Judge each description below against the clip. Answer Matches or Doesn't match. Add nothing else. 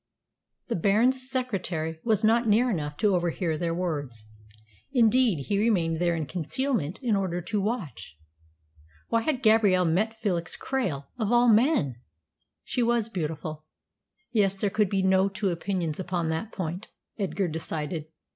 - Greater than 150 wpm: Doesn't match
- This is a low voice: Doesn't match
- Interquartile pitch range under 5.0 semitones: Doesn't match